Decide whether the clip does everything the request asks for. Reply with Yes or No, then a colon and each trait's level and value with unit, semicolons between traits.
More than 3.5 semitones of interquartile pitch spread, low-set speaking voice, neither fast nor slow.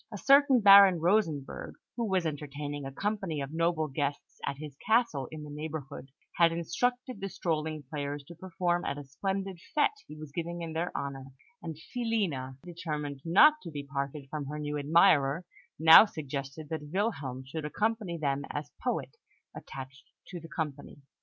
No: average, 4.6 semitones; medium, 155 Hz; average, 165 wpm